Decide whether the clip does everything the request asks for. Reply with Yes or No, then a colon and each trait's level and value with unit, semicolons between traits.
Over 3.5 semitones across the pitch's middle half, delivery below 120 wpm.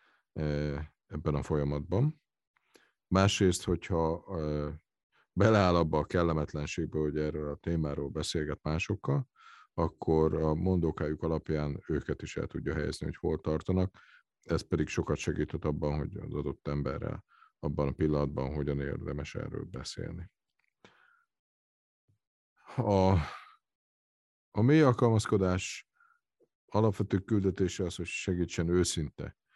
Yes: average, 3.9 semitones; average, 110 wpm